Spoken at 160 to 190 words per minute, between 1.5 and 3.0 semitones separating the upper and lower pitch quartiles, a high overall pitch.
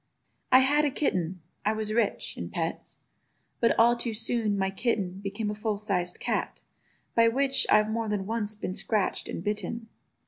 Yes: average, 165 wpm; narrow, 2.6 semitones; high, 215 Hz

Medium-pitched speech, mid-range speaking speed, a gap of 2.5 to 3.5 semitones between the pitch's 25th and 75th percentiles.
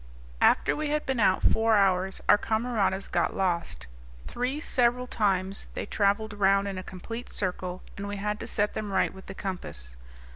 No: high, 200 Hz; average, 180 wpm; average, 2.9 semitones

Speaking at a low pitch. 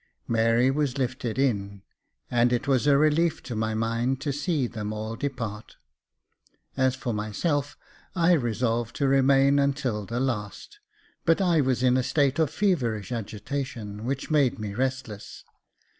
Yes: low, 130 Hz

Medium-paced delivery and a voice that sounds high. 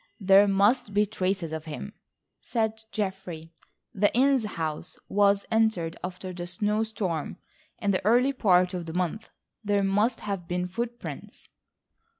Yes: average, 145 wpm; high, 200 Hz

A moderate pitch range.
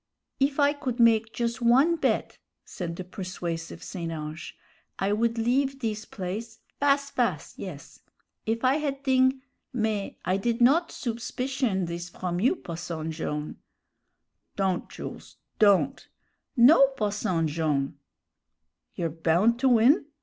No: wide, 6.9 semitones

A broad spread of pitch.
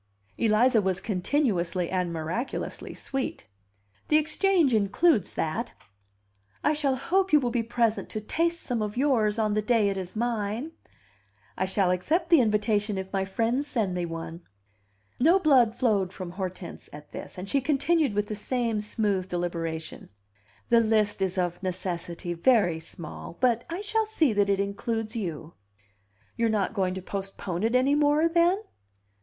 Yes: wide, 5.7 semitones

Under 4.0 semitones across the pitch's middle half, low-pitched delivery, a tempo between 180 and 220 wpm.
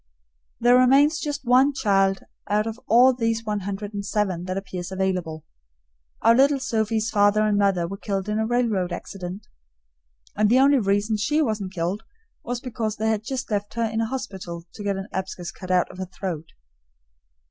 No: average, 3.5 semitones; high, 210 Hz; average, 185 wpm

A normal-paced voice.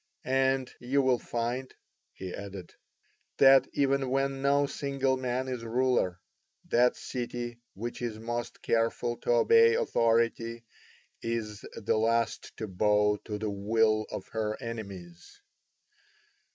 No: slow, 125 wpm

